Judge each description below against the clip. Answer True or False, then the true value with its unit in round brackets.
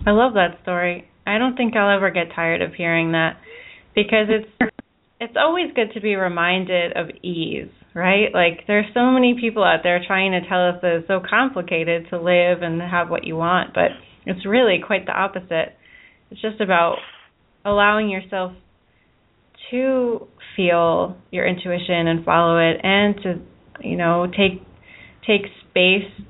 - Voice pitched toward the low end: False (185 Hz)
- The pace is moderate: True (165 wpm)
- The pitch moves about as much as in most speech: True (3.5 semitones)